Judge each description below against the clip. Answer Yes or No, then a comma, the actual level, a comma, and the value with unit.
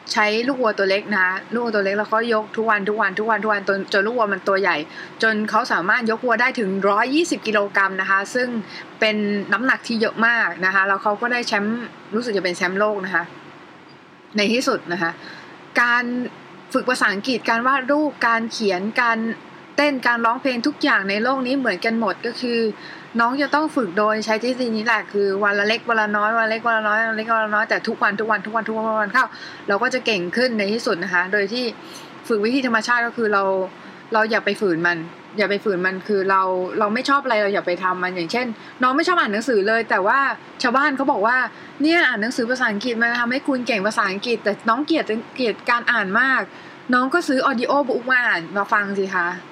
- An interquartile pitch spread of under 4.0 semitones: Yes, average, 3.2 semitones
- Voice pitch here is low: No, high, 220 Hz